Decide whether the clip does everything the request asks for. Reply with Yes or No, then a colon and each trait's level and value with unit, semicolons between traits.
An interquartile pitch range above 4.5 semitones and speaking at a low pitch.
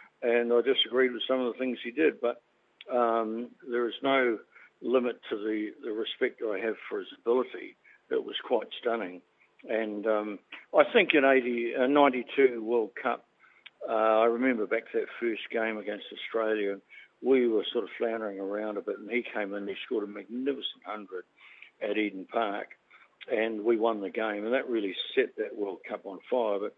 Yes: average, 5.2 semitones; low, 120 Hz